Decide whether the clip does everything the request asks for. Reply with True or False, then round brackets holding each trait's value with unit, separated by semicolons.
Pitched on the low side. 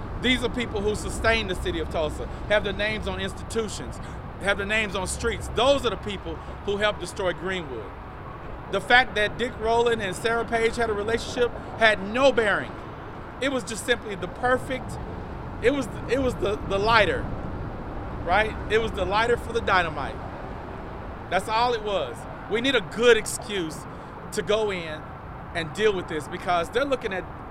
False (215 Hz)